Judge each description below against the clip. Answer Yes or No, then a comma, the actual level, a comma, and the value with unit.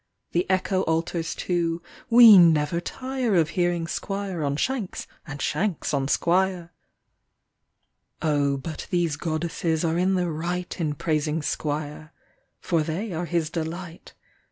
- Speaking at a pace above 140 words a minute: No, slow, 135 wpm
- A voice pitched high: No, medium, 170 Hz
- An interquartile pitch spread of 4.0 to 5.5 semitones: No, narrow, 2.6 semitones